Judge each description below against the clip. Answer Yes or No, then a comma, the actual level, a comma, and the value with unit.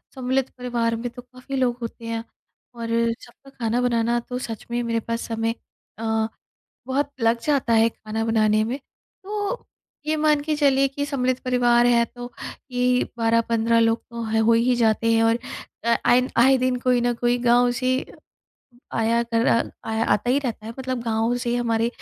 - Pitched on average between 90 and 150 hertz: No, high, 240 Hz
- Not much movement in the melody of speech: Yes, narrow, 1.8 semitones